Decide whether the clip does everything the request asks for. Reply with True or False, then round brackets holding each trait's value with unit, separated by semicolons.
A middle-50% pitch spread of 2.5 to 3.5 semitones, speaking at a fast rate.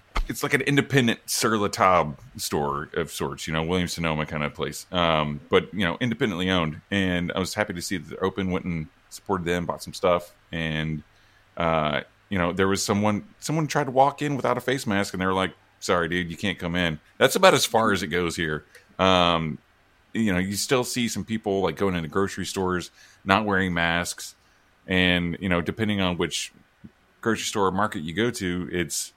True (3.0 semitones; 210 wpm)